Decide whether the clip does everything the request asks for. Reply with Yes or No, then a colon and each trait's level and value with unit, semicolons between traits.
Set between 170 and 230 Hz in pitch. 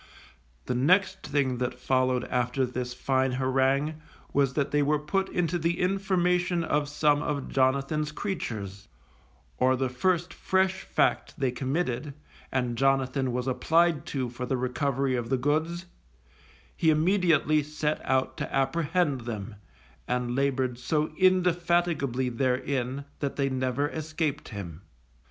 No: medium, 140 Hz